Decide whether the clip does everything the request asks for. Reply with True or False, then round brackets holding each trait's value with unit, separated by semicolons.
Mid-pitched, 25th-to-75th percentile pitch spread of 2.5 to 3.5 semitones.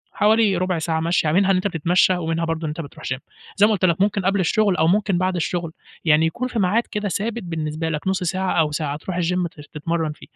True (175 Hz; 3.2 semitones)